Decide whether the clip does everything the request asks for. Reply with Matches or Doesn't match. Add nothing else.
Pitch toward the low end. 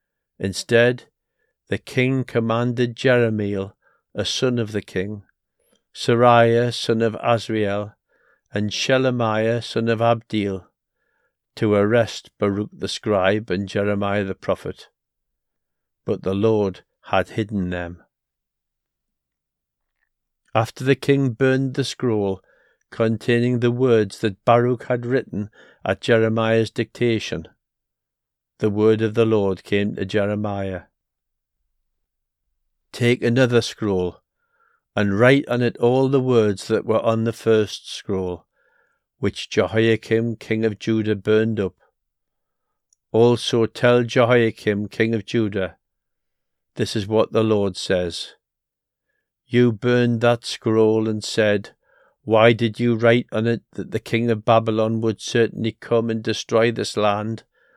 Matches